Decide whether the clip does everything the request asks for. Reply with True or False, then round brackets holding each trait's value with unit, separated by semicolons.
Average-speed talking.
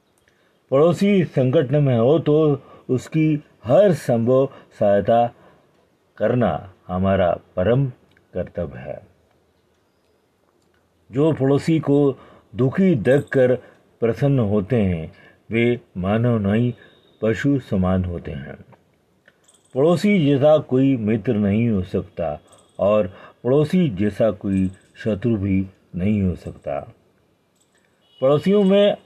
False (100 wpm)